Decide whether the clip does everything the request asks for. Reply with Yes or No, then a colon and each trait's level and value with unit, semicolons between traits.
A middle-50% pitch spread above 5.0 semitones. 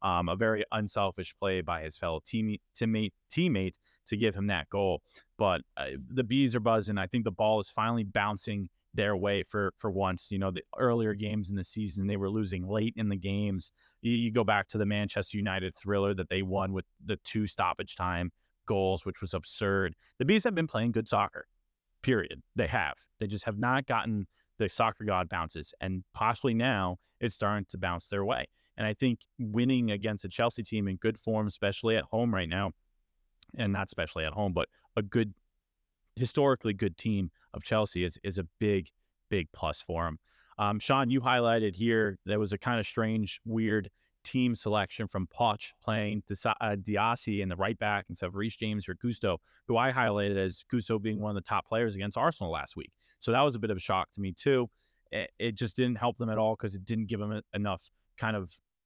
No: average, 2.8 semitones